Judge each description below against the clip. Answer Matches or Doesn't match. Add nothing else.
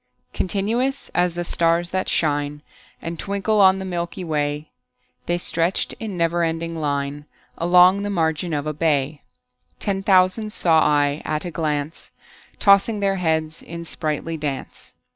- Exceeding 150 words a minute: Doesn't match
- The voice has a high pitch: Doesn't match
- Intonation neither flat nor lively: Matches